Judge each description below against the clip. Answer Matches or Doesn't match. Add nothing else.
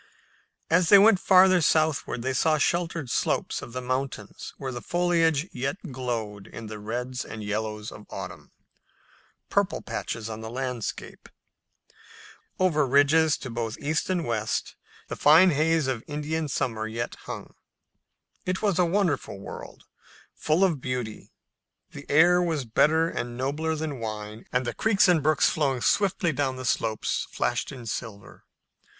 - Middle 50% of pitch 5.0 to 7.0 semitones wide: Matches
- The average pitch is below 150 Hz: Matches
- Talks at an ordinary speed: Matches